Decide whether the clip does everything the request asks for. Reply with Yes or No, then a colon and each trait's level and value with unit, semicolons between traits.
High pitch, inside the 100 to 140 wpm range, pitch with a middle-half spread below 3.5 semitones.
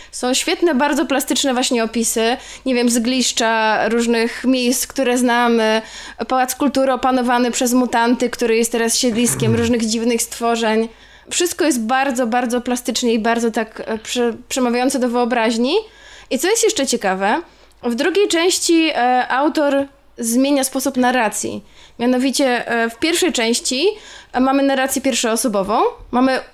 Yes: very high, 250 Hz; average, 130 wpm; average, 2.8 semitones